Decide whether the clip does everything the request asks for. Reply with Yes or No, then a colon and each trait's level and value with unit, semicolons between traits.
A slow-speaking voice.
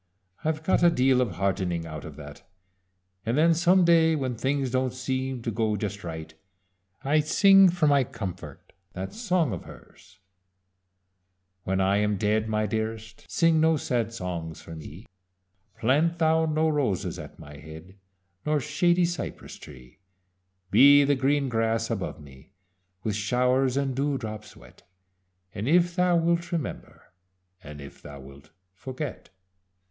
No: average, 150 wpm